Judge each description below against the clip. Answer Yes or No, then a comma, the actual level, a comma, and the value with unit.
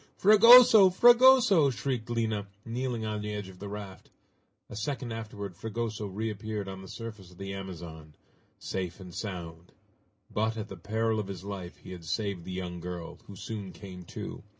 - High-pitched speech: No, low, 105 Hz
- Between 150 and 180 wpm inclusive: Yes, average, 175 wpm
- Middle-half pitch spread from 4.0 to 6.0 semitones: No, average, 3.3 semitones